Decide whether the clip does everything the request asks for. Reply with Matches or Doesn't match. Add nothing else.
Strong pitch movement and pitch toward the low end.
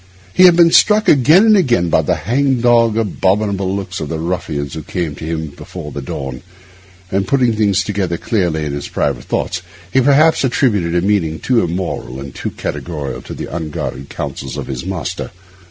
Matches